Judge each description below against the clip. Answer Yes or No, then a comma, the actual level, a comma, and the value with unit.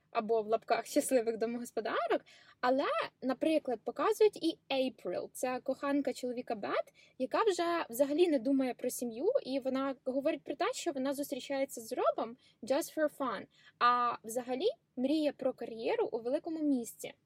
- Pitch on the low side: No, very high, 265 Hz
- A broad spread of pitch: No, average, 3.4 semitones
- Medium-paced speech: Yes, average, 145 wpm